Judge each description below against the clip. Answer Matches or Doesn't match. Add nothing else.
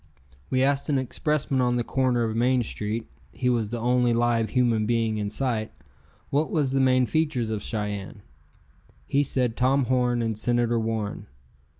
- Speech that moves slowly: Doesn't match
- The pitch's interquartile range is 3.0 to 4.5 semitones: Doesn't match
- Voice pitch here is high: Doesn't match